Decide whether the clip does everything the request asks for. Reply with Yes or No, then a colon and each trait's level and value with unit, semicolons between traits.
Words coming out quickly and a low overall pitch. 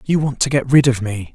Yes: fast, 310 wpm; low, 130 Hz